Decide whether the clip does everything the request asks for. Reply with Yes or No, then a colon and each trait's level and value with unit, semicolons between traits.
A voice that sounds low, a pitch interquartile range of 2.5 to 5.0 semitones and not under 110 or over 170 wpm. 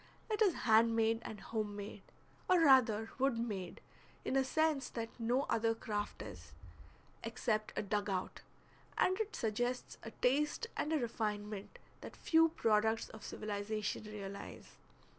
No: high, 225 Hz; average, 3.9 semitones; average, 145 wpm